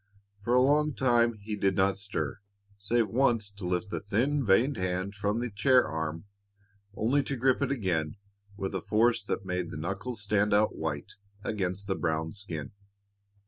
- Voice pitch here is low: Yes, low, 100 Hz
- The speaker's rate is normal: Yes, average, 175 wpm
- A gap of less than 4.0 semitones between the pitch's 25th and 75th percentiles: No, average, 4.4 semitones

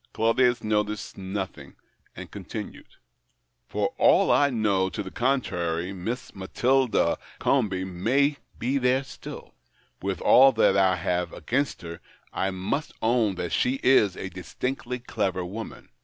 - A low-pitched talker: Yes, low, 105 Hz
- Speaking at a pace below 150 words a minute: Yes, average, 140 wpm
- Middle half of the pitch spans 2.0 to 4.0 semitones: No, average, 5.1 semitones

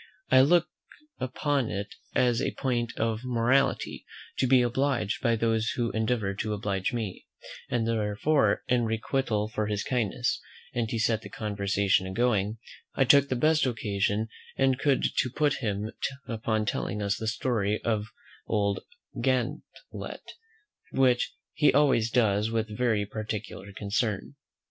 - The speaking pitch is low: Yes, low, 115 Hz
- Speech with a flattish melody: No, average, 3.3 semitones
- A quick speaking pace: No, average, 145 wpm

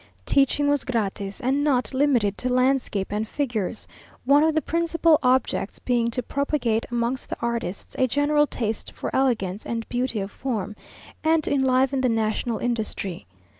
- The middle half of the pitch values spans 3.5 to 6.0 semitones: Yes, average, 4.0 semitones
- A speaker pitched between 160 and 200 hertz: No, very high, 250 Hz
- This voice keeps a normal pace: Yes, average, 160 wpm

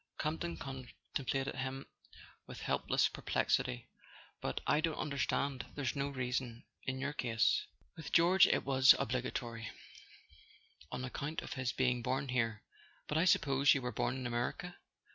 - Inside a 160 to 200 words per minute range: No, average, 145 wpm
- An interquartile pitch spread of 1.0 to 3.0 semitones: Yes, narrow, 2.5 semitones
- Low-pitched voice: Yes, low, 130 Hz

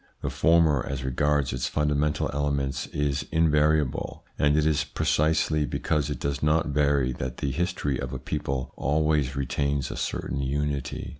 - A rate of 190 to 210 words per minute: No, average, 160 wpm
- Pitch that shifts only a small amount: Yes, narrow, 1.8 semitones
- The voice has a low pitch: Yes, very low, 75 Hz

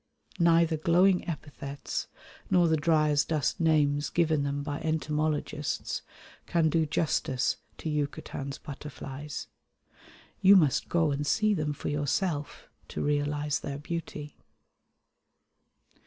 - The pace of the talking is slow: Yes, slow, 115 wpm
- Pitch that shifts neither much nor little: No, narrow, 2.2 semitones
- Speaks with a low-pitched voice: No, medium, 150 Hz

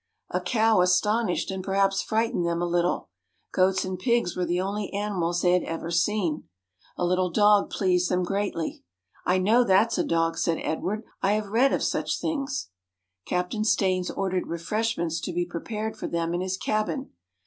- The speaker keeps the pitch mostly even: No, average, 3.3 semitones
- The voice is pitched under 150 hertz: No, medium, 185 Hz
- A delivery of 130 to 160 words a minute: No, average, 175 wpm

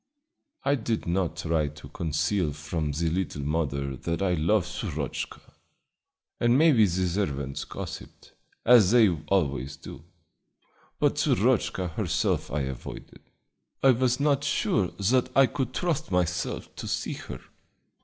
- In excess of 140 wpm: No, slow, 135 wpm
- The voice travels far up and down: Yes, wide, 7.3 semitones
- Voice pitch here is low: Yes, very low, 90 Hz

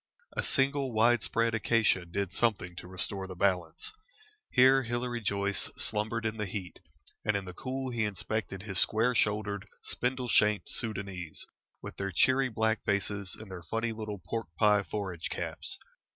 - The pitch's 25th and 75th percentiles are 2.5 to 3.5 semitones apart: Yes, average, 3.0 semitones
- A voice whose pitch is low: Yes, low, 105 Hz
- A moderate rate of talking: Yes, average, 160 wpm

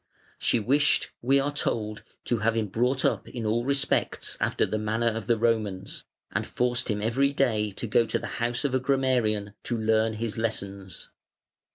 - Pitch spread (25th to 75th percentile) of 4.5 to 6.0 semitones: No, narrow, 2.6 semitones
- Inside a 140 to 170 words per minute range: No, average, 185 wpm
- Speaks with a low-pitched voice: Yes, low, 115 Hz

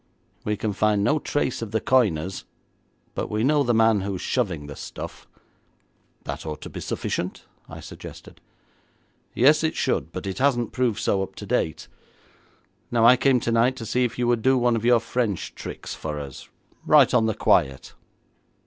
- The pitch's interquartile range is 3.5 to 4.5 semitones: Yes, average, 4.1 semitones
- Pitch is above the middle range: No, low, 115 Hz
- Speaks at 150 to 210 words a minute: Yes, average, 185 wpm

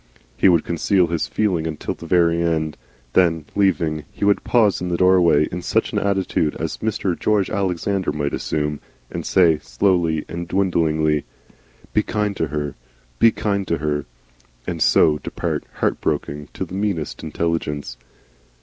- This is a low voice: Yes, very low, 85 Hz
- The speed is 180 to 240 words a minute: No, average, 155 wpm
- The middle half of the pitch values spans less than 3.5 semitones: No, average, 3.8 semitones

